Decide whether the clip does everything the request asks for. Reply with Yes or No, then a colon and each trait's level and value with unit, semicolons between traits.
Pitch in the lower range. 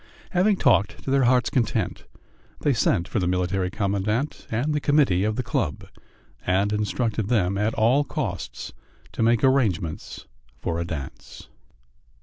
Yes: low, 110 Hz